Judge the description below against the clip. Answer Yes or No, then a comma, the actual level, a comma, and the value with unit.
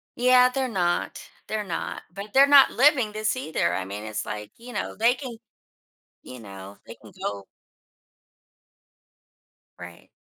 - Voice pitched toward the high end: Yes, high, 215 Hz